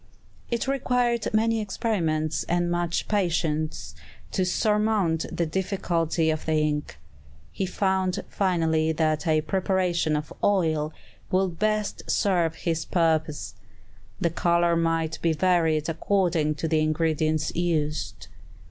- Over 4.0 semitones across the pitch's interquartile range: No, average, 3.2 semitones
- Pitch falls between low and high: Yes, medium, 170 Hz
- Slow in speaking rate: Yes, slow, 120 wpm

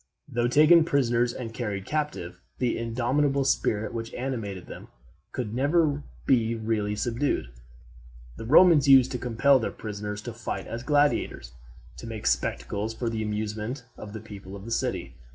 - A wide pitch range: No, average, 4.0 semitones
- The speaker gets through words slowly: No, average, 160 wpm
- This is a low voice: Yes, low, 115 Hz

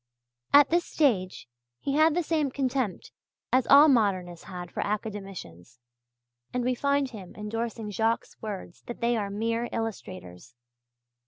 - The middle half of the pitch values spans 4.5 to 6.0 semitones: Yes, wide, 5.4 semitones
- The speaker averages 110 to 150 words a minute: Yes, average, 140 wpm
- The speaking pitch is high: Yes, high, 225 Hz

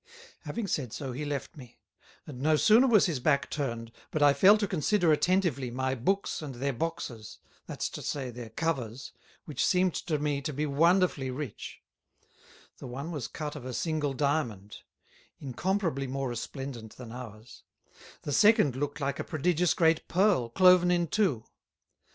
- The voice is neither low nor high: Yes, medium, 145 Hz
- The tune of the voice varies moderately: Yes, average, 5.0 semitones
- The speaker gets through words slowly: No, average, 165 wpm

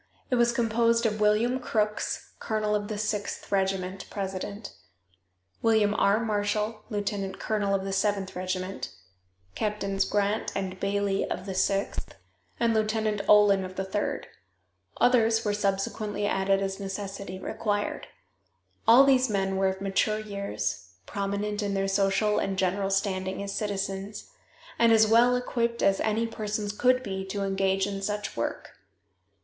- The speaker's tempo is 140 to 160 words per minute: Yes, average, 145 wpm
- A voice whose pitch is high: Yes, high, 205 Hz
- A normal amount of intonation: No, narrow, 1.9 semitones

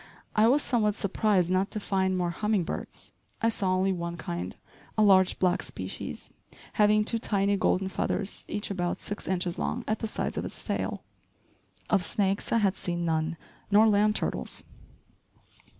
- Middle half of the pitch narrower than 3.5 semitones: Yes, average, 2.7 semitones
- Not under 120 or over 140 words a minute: No, average, 165 wpm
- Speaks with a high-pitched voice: Yes, high, 195 Hz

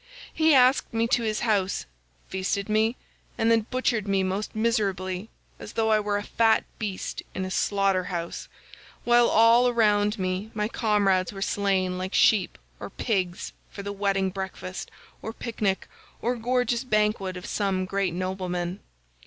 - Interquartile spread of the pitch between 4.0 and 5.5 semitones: No, average, 3.0 semitones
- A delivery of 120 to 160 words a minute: Yes, average, 155 wpm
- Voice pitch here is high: Yes, high, 205 Hz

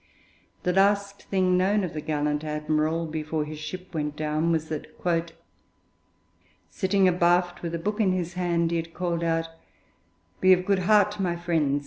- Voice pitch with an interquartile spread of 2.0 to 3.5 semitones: Yes, average, 2.9 semitones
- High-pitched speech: No, medium, 170 Hz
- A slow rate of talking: No, average, 165 wpm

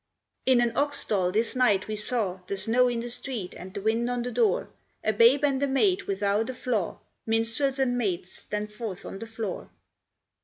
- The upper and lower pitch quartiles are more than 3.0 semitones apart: Yes, average, 3.4 semitones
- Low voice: No, high, 225 Hz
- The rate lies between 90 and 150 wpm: No, average, 200 wpm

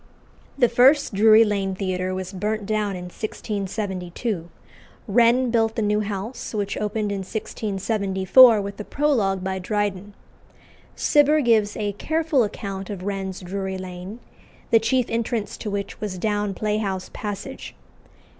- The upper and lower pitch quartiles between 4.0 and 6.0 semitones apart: No, average, 2.7 semitones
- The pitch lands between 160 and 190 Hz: No, high, 205 Hz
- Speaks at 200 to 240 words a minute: No, slow, 135 wpm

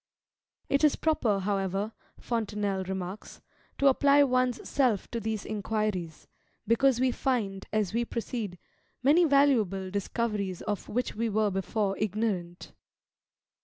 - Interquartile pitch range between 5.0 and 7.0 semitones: No, average, 4.2 semitones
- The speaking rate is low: Yes, slow, 125 wpm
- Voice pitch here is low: No, high, 215 Hz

